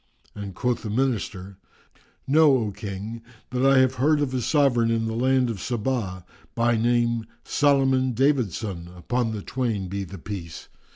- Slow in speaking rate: No, average, 165 wpm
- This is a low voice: Yes, low, 115 Hz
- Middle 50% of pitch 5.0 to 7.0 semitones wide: No, average, 4.3 semitones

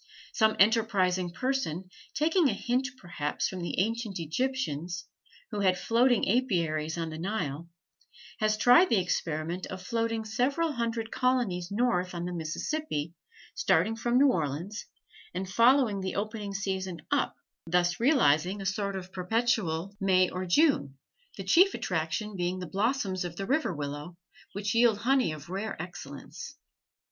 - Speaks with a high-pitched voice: Yes, high, 195 Hz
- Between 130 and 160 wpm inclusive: Yes, average, 145 wpm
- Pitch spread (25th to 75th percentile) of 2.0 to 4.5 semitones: No, average, 5.0 semitones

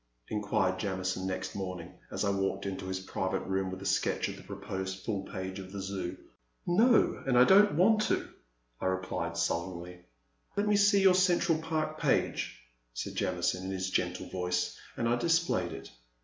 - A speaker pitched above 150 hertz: No, very low, 95 Hz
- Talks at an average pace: Yes, average, 180 wpm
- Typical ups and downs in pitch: No, wide, 8.8 semitones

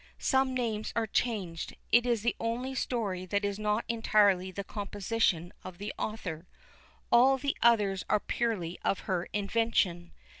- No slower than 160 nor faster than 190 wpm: No, average, 150 wpm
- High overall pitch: Yes, high, 210 Hz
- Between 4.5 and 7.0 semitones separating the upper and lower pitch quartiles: No, average, 3.7 semitones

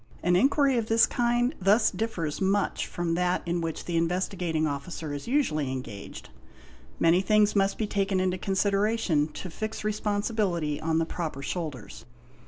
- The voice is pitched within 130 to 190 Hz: Yes, medium, 185 Hz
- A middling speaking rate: Yes, average, 155 wpm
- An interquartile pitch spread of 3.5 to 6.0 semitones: Yes, average, 4.5 semitones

